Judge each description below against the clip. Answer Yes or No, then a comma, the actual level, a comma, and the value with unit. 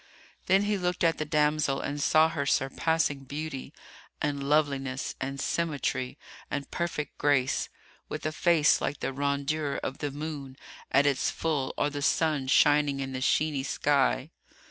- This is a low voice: No, medium, 145 Hz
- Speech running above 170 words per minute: No, average, 155 wpm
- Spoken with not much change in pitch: Yes, narrow, 2.2 semitones